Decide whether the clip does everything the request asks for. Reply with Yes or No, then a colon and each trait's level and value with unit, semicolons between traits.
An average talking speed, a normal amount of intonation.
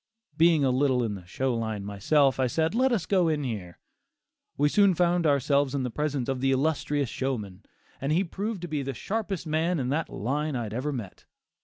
No: fast, 210 wpm; average, 4.4 semitones